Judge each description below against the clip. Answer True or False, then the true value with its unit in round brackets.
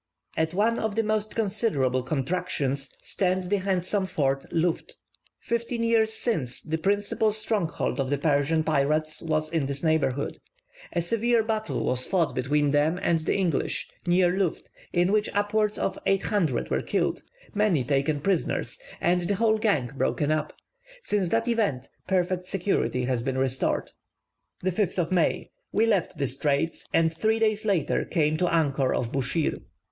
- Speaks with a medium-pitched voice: True (175 Hz)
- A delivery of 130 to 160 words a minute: True (155 wpm)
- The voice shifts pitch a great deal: True (6.1 semitones)